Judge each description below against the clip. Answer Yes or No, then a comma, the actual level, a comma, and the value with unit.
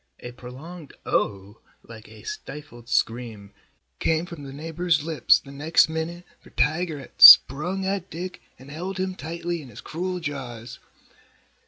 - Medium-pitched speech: Yes, medium, 155 Hz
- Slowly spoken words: No, average, 150 wpm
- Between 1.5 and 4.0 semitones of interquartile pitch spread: No, wide, 5.4 semitones